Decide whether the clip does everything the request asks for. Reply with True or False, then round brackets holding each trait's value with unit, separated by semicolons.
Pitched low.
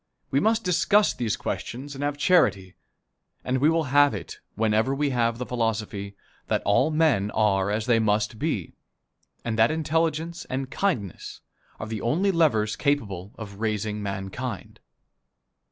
True (120 Hz)